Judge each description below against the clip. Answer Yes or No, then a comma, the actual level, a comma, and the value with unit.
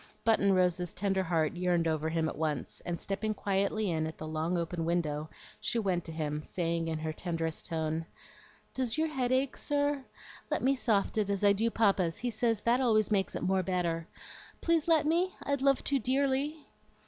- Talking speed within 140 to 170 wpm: No, average, 195 wpm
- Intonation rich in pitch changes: Yes, wide, 6.9 semitones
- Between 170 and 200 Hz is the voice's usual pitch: Yes, high, 190 Hz